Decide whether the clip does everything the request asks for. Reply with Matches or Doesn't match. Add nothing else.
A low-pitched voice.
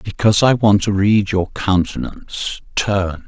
Matches